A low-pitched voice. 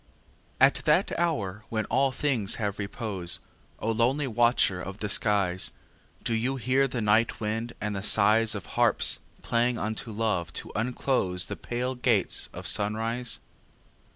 Yes: low, 110 Hz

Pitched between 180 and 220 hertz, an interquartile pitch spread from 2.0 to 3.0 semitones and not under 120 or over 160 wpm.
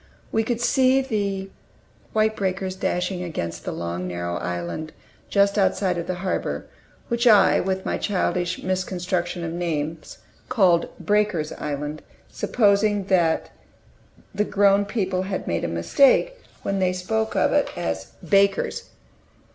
No: high, 190 Hz; average, 3.4 semitones; slow, 135 wpm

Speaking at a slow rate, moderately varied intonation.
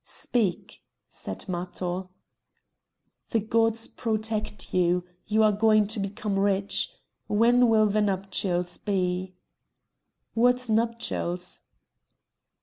Yes: slow, 95 wpm; average, 3.1 semitones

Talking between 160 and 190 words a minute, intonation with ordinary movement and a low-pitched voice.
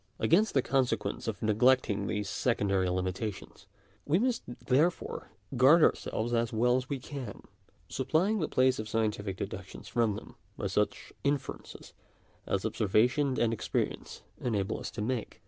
No: average, 145 wpm; average, 4.1 semitones; low, 120 Hz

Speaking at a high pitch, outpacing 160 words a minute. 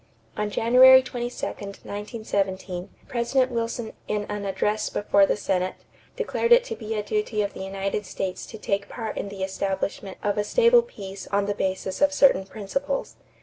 Yes: high, 210 Hz; average, 170 wpm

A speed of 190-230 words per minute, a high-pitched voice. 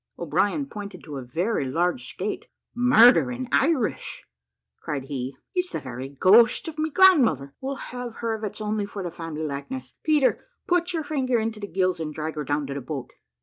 Yes: average, 195 wpm; high, 200 Hz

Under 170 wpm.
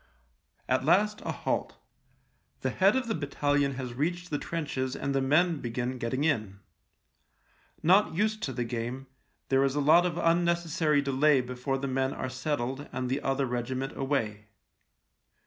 Yes: average, 160 wpm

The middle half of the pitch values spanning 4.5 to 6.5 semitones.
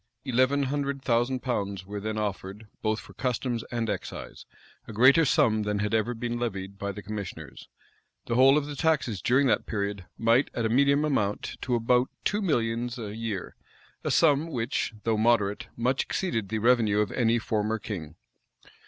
No: average, 3.6 semitones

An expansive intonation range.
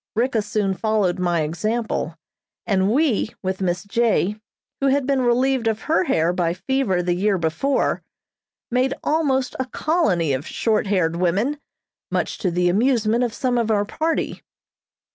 Yes: wide, 6.1 semitones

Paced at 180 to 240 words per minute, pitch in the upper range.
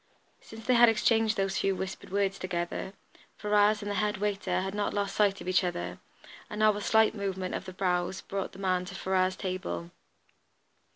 Yes: average, 190 wpm; high, 195 Hz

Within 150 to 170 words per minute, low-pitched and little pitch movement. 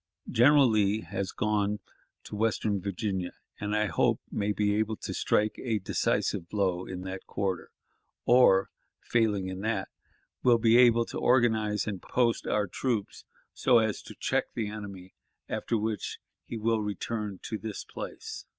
Yes: average, 155 wpm; low, 105 Hz; narrow, 2.3 semitones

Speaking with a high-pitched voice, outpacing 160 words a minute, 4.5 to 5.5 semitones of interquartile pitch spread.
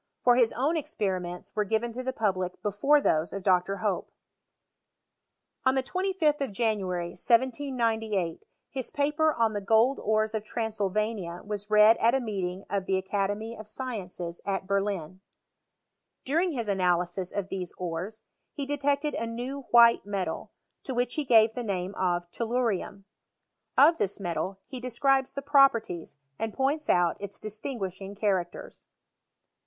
No: high, 215 Hz; average, 150 wpm; average, 5.0 semitones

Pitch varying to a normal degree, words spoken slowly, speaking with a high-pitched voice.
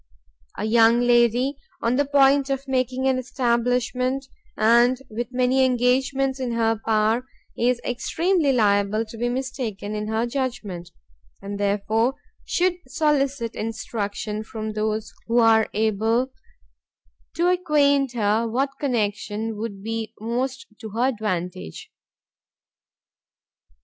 Yes: average, 3.3 semitones; slow, 120 wpm; high, 235 Hz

